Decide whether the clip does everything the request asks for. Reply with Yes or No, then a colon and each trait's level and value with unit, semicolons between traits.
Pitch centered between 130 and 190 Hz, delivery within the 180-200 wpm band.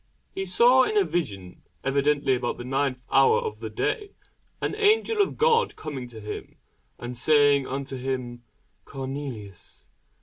No: medium, 140 Hz; average, 155 wpm